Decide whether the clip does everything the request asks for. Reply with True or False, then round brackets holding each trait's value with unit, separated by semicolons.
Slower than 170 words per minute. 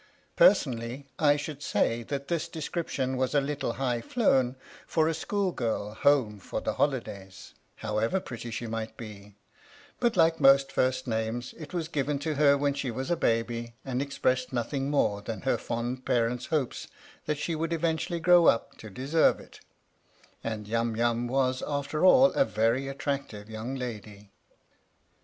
True (160 wpm)